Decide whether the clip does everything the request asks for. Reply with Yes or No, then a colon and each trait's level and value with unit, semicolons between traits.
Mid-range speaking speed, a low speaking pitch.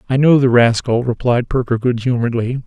Yes: average, 180 wpm; low, 125 Hz